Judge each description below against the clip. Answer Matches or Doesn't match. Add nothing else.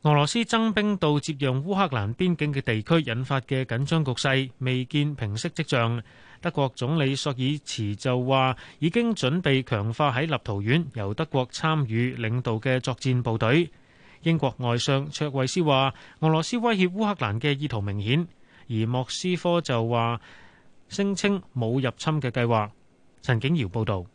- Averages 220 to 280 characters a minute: Matches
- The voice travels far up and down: Doesn't match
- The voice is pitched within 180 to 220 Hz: Doesn't match